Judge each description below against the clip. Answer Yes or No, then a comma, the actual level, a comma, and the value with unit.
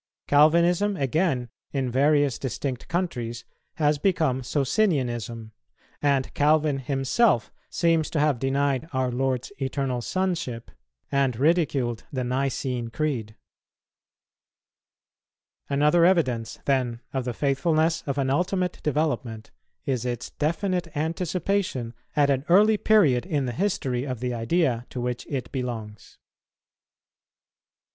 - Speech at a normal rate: No, slow, 115 wpm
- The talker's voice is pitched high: No, medium, 140 Hz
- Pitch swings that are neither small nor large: Yes, average, 4.5 semitones